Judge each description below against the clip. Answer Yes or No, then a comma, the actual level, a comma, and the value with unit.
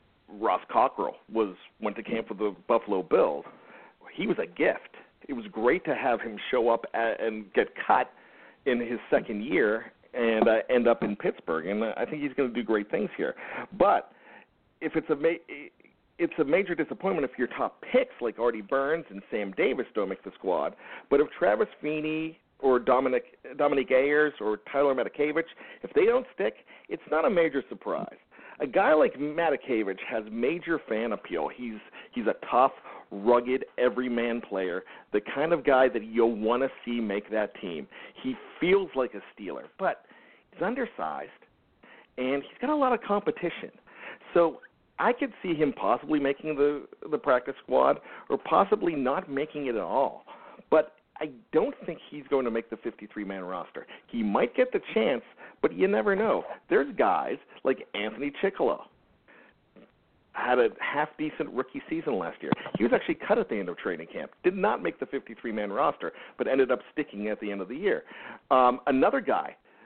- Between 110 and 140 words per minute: No, average, 180 wpm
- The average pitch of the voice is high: No, low, 135 Hz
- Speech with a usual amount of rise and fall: No, wide, 5.8 semitones